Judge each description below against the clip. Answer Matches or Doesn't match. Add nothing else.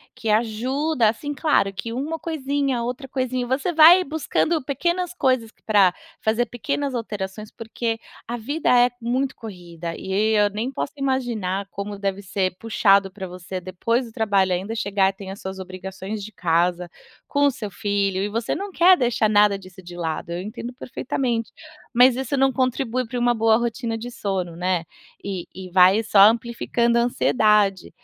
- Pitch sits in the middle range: Doesn't match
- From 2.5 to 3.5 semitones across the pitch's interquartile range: Doesn't match